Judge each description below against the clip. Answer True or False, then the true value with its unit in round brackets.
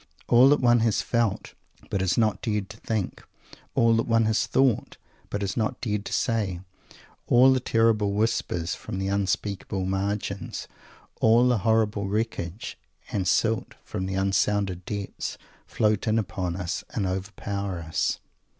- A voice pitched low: True (105 Hz)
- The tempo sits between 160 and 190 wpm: False (150 wpm)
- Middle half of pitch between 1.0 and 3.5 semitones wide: True (2.8 semitones)